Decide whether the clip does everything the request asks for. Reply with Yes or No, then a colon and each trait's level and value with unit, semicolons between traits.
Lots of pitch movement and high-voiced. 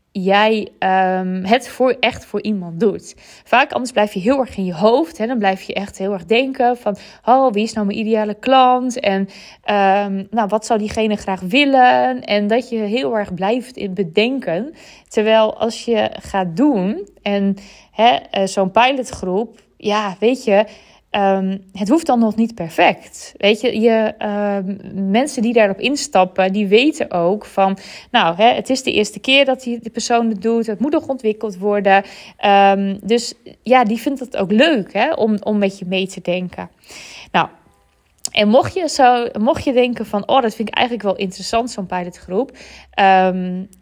No: average, 3.4 semitones; high, 215 Hz